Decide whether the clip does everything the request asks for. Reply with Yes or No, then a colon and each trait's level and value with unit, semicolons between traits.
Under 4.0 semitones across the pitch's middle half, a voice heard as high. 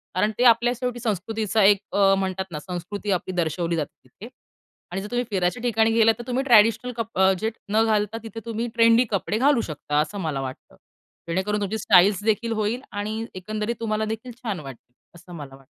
Yes: average, 3.5 semitones; high, 210 Hz